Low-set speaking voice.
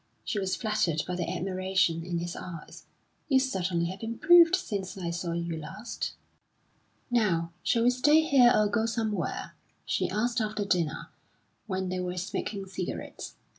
No: high, 190 Hz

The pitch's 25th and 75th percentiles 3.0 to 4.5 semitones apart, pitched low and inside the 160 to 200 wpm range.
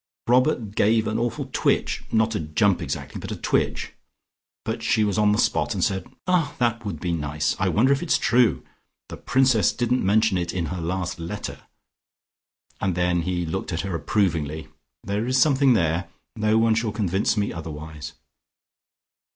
No: average, 5.0 semitones; low, 100 Hz; average, 175 wpm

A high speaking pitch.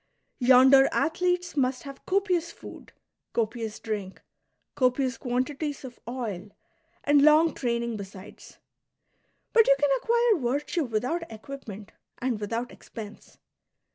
Yes: very high, 255 Hz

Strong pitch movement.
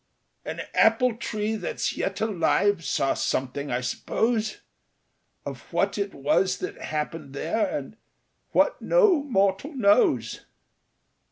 Yes: wide, 7.2 semitones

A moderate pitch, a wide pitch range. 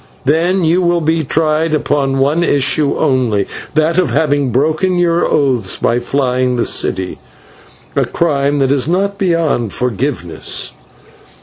No: medium, 145 Hz; average, 4.3 semitones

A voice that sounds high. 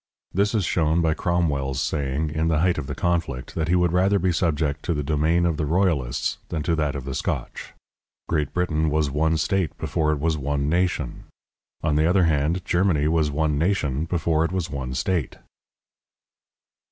No: very low, 80 Hz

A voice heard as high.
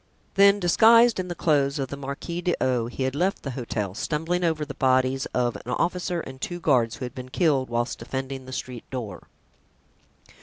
No: low, 135 Hz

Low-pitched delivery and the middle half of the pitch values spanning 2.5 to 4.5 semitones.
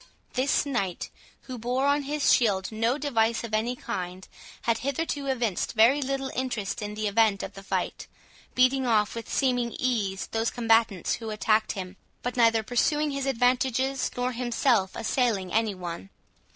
No: high, 235 Hz; average, 3.4 semitones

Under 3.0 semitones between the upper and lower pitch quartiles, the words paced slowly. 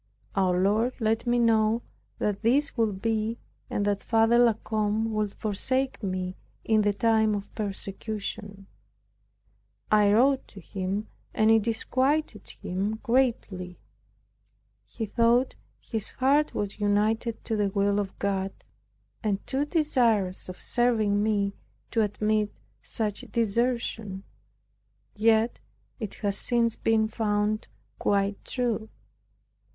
Yes: narrow, 2.4 semitones; slow, 120 wpm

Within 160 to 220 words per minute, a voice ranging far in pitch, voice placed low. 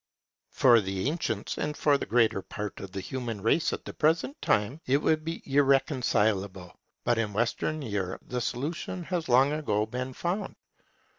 Yes: average, 165 wpm; wide, 6.3 semitones; low, 125 Hz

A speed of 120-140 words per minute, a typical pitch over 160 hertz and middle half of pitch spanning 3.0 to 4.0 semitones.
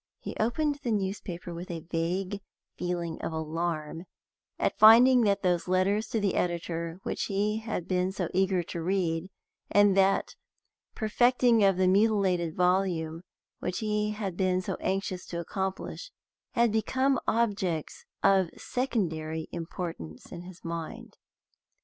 Yes: slow, 135 wpm; medium, 185 Hz; average, 3.6 semitones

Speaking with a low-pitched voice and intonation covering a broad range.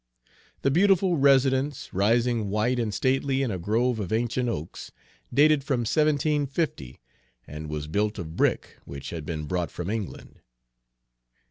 Yes: low, 120 Hz; wide, 7.1 semitones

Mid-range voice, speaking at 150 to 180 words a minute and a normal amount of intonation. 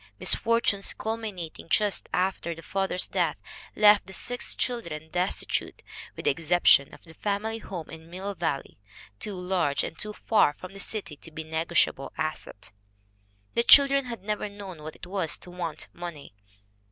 Yes: medium, 180 Hz; average, 165 wpm; average, 4.4 semitones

